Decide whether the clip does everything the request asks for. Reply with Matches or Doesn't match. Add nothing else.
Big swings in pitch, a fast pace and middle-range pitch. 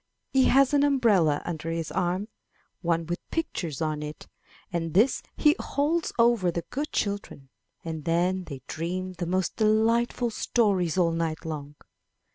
Doesn't match